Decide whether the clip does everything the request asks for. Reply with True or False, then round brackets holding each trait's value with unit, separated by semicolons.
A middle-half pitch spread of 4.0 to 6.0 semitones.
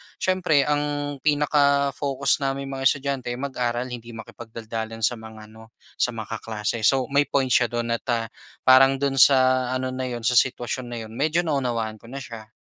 False (3.2 semitones)